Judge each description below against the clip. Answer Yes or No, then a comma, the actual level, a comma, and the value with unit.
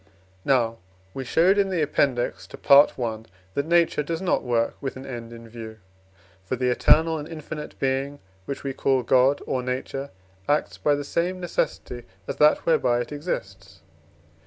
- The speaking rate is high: No, average, 170 wpm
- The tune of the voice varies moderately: Yes, average, 3.8 semitones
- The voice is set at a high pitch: No, low, 135 Hz